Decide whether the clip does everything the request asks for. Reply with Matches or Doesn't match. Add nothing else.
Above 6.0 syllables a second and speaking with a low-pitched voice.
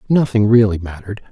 Matches